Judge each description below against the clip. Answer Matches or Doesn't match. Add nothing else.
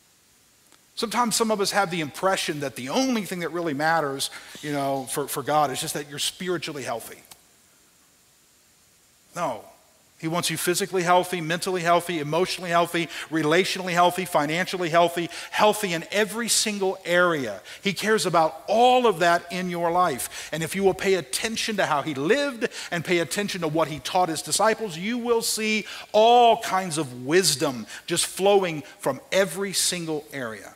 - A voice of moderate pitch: Matches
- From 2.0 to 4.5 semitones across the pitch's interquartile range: Matches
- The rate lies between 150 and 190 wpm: Matches